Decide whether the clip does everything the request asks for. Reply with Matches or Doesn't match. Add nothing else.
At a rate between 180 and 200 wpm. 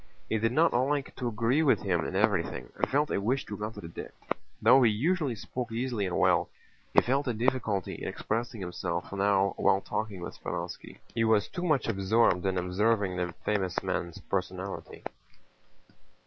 Doesn't match